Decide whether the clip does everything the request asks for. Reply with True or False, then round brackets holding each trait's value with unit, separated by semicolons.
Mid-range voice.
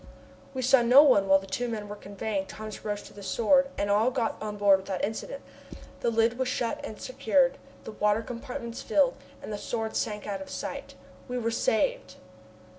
False (225 Hz)